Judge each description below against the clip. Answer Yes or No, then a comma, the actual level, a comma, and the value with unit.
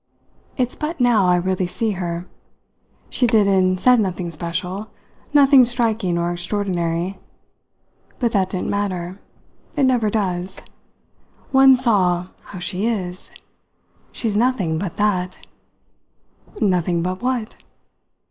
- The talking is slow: Yes, slow, 120 wpm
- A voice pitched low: No, high, 195 Hz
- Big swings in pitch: No, average, 4.4 semitones